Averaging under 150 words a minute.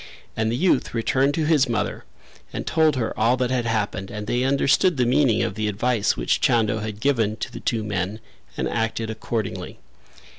No: average, 190 wpm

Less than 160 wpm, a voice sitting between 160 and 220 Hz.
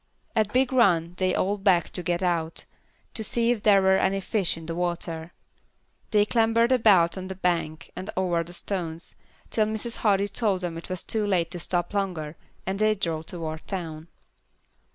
No: average, 185 wpm; medium, 185 Hz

